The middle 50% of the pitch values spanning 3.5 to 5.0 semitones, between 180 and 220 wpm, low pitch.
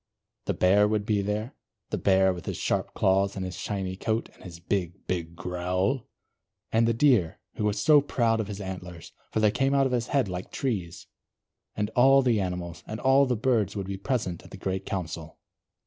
Yes: average, 4.0 semitones; fast, 205 wpm; low, 100 Hz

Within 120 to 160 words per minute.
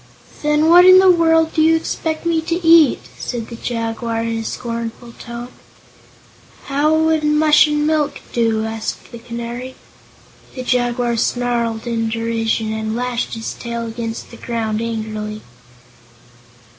Yes: average, 145 wpm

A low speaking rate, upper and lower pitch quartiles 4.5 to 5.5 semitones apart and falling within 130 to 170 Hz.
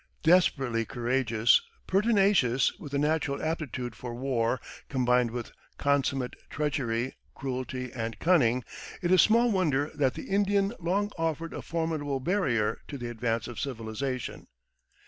Yes: slow, 130 wpm; average, 5.1 semitones; low, 135 Hz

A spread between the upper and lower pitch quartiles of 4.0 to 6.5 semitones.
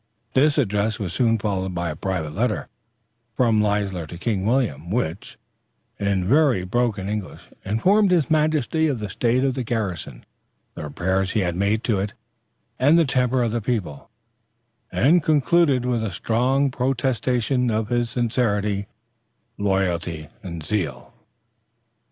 Yes: average, 4.9 semitones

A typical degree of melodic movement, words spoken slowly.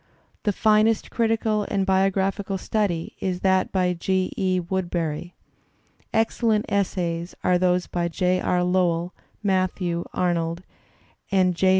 No: narrow, 1.9 semitones; slow, 120 wpm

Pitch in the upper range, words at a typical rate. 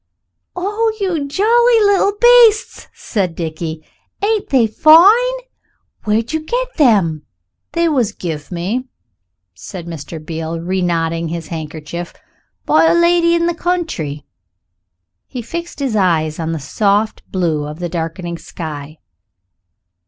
No: high, 200 Hz; slow, 130 wpm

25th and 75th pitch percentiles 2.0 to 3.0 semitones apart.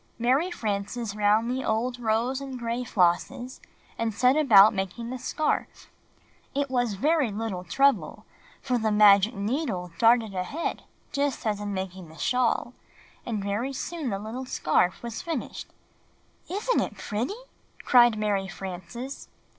No: average, 4.2 semitones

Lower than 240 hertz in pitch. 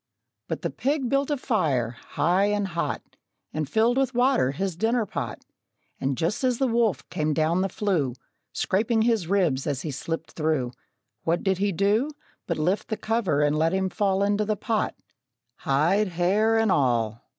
Yes: high, 190 Hz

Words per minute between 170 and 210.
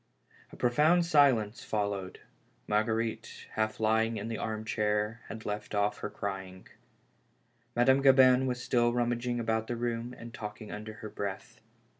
No: average, 140 wpm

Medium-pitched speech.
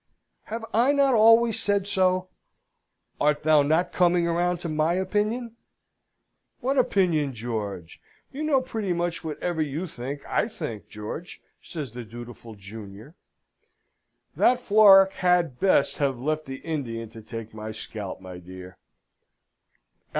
Yes: medium, 155 Hz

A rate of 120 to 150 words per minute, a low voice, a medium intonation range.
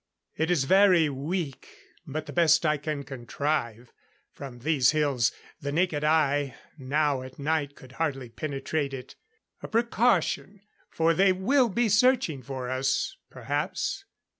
No: average, 140 wpm; medium, 150 Hz; average, 4.7 semitones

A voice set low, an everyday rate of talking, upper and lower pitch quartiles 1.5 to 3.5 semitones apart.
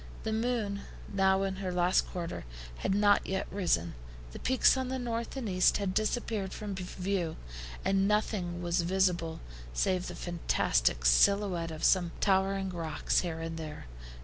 No: high, 190 Hz; average, 155 wpm; average, 2.8 semitones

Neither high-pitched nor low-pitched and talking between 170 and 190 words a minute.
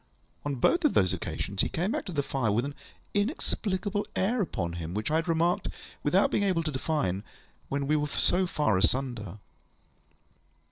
Yes: medium, 150 Hz; average, 180 wpm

